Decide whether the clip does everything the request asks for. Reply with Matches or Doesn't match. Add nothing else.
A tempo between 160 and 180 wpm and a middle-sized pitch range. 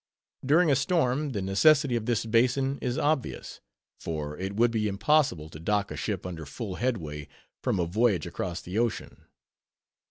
Doesn't match